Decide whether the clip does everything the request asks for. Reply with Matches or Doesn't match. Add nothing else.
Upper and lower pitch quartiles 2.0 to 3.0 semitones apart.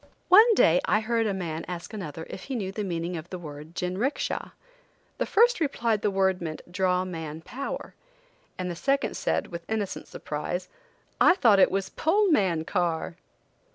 Doesn't match